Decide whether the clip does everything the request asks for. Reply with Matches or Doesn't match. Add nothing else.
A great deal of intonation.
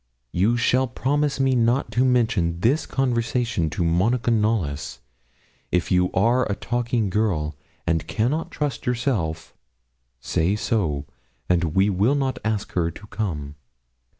Matches